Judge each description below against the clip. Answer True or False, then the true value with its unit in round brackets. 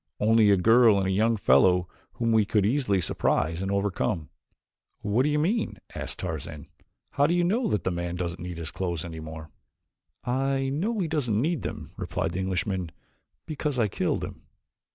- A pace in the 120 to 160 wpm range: False (185 wpm)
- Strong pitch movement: True (7.2 semitones)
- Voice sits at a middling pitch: False (105 Hz)